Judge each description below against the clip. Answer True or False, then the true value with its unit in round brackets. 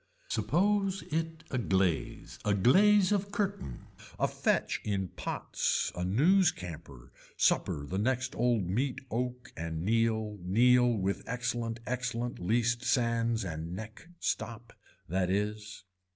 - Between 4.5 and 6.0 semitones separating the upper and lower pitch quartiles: True (4.9 semitones)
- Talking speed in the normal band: False (125 wpm)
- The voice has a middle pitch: False (115 Hz)